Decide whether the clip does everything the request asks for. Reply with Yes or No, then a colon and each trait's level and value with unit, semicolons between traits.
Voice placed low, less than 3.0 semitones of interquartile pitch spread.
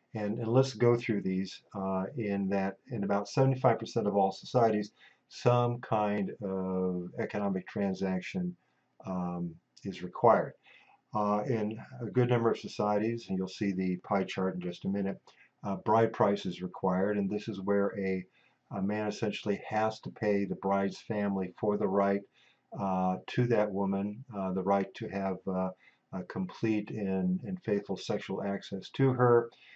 Yes: low, 100 Hz; narrow, 2.4 semitones